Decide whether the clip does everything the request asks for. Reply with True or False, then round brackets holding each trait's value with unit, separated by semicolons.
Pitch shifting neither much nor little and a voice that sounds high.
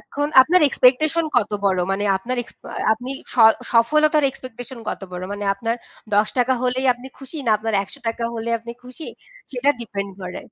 True (3.1 semitones; 245 Hz)